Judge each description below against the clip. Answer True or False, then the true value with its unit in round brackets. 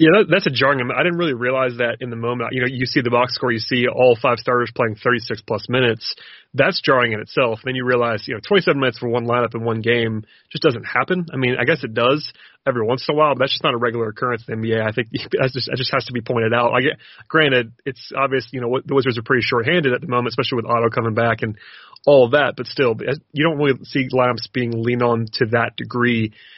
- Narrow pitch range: True (2.3 semitones)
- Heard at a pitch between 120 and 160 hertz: True (125 Hz)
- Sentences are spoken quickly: True (270 wpm)